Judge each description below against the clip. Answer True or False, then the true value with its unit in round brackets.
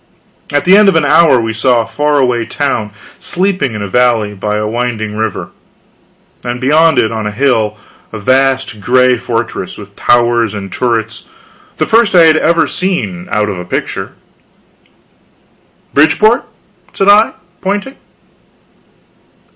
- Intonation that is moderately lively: False (6.3 semitones)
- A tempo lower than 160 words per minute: True (145 wpm)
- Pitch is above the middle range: False (125 Hz)